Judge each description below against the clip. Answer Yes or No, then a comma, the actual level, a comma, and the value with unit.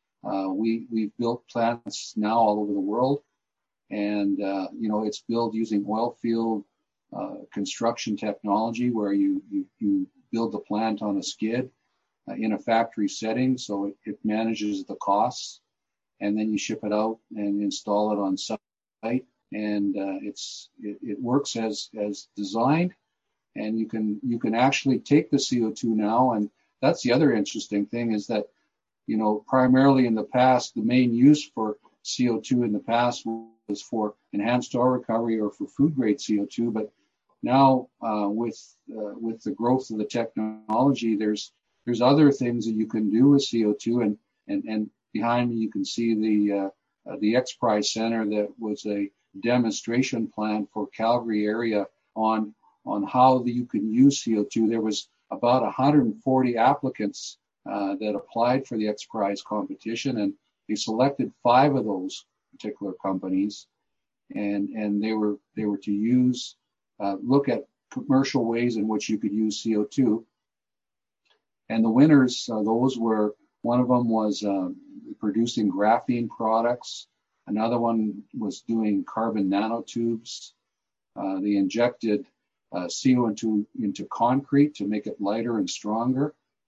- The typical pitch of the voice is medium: No, low, 115 Hz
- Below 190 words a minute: Yes, average, 160 wpm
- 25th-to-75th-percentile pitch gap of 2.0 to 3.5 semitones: Yes, average, 2.9 semitones